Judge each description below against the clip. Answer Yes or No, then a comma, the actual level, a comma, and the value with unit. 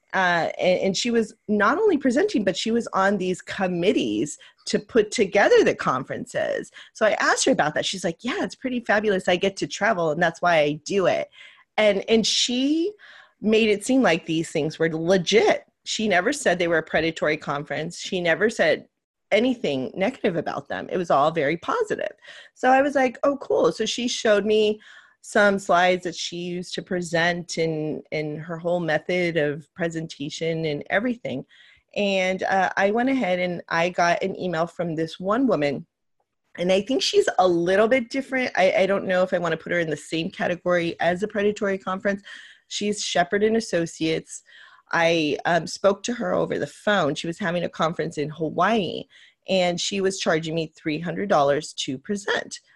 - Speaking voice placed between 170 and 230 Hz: Yes, medium, 185 Hz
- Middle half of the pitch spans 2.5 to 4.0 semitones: No, average, 4.6 semitones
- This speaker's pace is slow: No, average, 190 wpm